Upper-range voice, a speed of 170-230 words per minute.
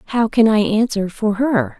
Yes: high, 210 Hz; average, 200 wpm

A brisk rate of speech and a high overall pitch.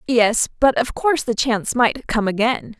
No: average, 195 wpm; high, 235 Hz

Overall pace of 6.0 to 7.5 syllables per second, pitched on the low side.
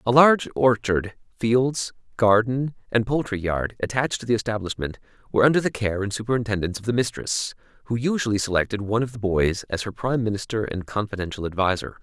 Yes: 6.2 syllables/s; low, 110 Hz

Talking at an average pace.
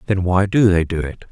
No: fast, 275 wpm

